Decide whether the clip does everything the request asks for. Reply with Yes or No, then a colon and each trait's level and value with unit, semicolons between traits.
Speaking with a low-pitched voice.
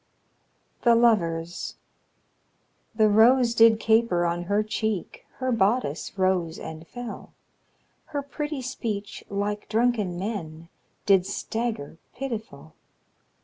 No: high, 215 Hz